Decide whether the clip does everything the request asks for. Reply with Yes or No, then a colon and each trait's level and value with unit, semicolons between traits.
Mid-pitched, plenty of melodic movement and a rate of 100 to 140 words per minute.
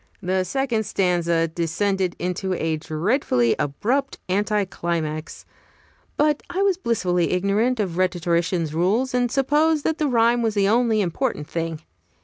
No: high, 195 Hz; wide, 6.4 semitones; slow, 135 wpm